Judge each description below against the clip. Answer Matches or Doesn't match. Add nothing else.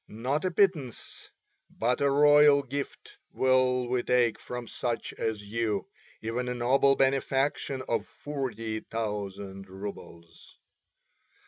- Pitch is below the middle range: Matches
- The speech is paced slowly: Matches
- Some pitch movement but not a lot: Matches